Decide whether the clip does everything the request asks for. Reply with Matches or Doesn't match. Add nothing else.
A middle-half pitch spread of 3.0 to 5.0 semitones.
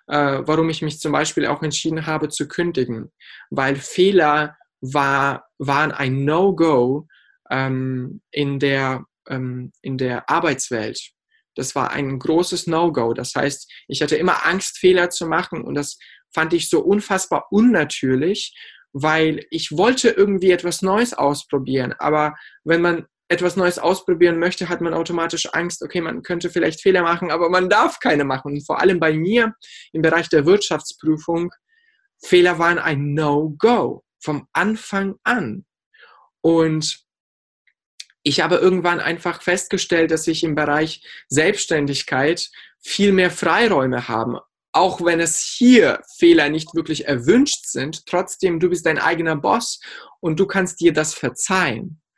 Matches